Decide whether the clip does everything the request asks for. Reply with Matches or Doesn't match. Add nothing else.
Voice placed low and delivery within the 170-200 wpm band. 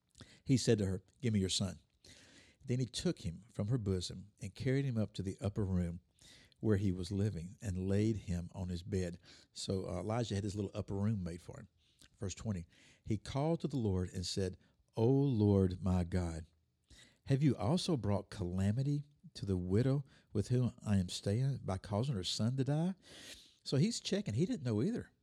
Matches